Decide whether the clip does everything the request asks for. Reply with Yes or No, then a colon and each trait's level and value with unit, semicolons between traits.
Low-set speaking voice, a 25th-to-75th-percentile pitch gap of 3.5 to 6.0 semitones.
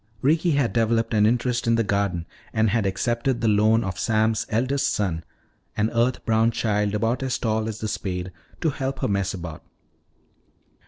No: low, 110 Hz; narrow, 2.6 semitones